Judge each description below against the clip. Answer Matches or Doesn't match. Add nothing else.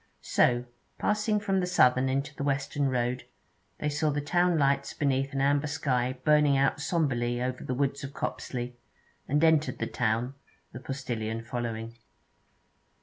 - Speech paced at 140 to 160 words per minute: Matches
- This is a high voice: Doesn't match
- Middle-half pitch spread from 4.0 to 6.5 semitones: Doesn't match